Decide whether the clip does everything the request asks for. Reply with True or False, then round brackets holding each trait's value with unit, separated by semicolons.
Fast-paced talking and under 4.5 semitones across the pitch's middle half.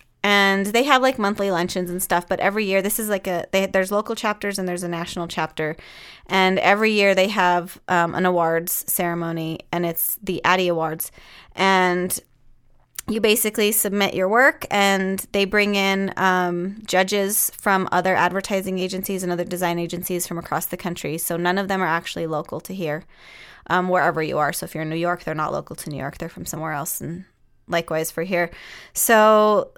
False (195 wpm; 2.5 semitones)